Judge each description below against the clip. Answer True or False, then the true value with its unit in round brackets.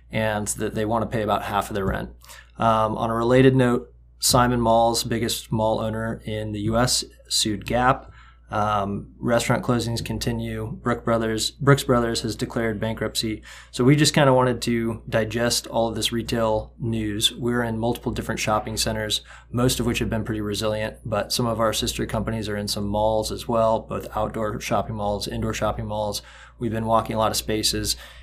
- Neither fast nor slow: True (185 wpm)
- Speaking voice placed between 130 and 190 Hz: False (110 Hz)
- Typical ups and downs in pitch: False (1.6 semitones)